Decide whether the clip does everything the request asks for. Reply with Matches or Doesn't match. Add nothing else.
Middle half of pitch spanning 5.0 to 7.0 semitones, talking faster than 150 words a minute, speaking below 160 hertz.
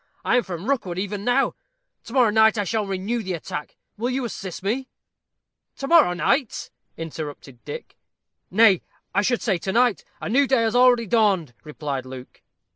Doesn't match